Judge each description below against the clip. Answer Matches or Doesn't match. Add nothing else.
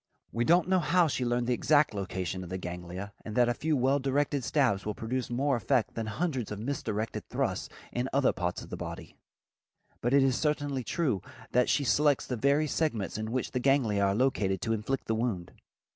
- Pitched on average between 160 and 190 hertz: Doesn't match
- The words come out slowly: Doesn't match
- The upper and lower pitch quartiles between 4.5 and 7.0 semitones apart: Matches